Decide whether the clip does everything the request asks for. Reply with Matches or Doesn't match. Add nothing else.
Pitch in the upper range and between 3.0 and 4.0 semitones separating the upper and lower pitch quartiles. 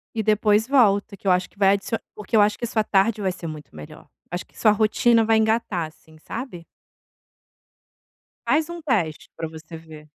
Doesn't match